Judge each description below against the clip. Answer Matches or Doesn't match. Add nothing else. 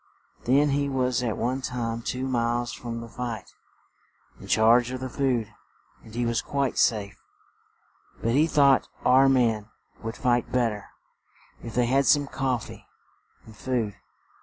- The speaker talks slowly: Doesn't match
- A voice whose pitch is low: Matches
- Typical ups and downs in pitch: Doesn't match